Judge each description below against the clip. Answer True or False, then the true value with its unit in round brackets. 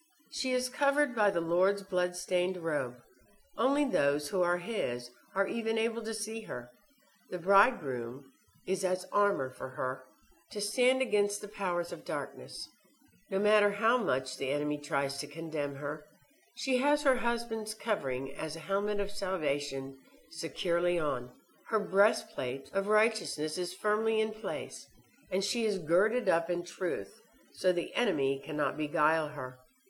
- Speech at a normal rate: True (155 wpm)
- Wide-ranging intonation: True (6.7 semitones)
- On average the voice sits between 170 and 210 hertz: True (185 Hz)